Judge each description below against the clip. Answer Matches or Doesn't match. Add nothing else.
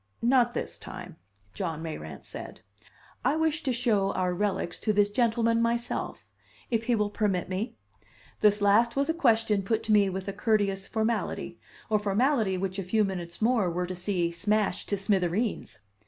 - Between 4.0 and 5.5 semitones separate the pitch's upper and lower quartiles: Doesn't match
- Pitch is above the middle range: Matches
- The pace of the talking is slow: Doesn't match